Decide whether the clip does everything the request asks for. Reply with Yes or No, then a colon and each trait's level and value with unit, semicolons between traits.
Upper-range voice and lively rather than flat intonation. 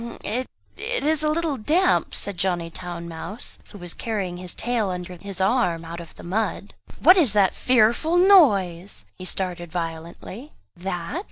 Yes: high, 195 Hz; wide, 6.5 semitones